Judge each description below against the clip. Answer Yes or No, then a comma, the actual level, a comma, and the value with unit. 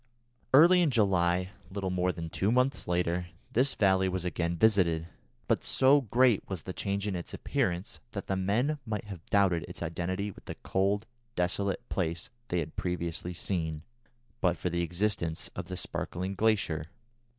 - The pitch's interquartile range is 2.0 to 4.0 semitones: Yes, average, 3.0 semitones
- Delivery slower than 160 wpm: No, average, 165 wpm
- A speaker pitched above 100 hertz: No, very low, 95 Hz